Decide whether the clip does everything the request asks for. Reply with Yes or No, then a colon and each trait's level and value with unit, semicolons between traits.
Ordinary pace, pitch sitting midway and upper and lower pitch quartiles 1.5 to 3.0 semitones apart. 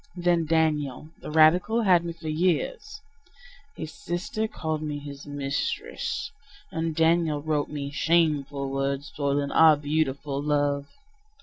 No: slow, 125 wpm; medium, 155 Hz; average, 2.7 semitones